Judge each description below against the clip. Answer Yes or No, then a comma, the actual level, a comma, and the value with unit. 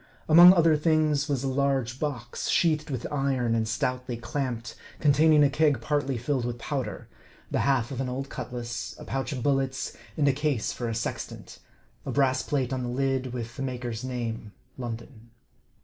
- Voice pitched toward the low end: Yes, low, 130 Hz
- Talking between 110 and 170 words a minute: No, average, 180 wpm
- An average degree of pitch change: Yes, average, 3.0 semitones